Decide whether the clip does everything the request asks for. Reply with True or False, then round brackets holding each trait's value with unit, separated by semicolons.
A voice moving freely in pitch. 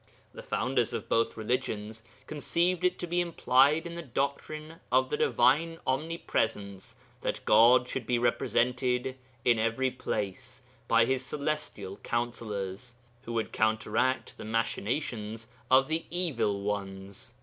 False (4.4 semitones)